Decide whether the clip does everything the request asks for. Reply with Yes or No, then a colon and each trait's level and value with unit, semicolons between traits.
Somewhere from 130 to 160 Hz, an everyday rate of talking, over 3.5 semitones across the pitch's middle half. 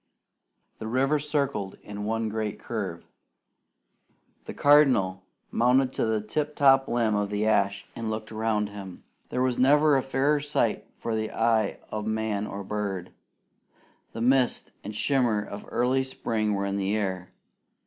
No: low, 110 Hz; average, 155 wpm; average, 4.2 semitones